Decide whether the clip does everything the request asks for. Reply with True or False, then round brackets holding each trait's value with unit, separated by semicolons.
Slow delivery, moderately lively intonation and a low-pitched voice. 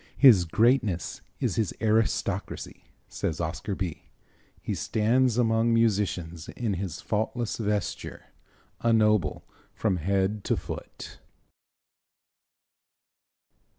True (95 wpm; 3.4 semitones; 105 Hz)